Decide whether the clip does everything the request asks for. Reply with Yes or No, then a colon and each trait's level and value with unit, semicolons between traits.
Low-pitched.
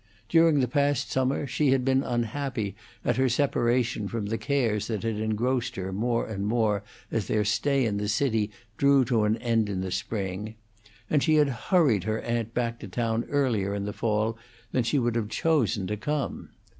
Yes: low, 115 Hz